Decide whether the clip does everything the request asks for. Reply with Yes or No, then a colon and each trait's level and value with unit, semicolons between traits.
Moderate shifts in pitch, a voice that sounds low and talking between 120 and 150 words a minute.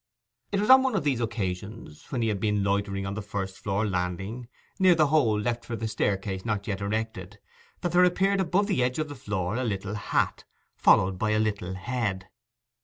No: average, 4.6 semitones; low, 110 Hz; fast, 205 wpm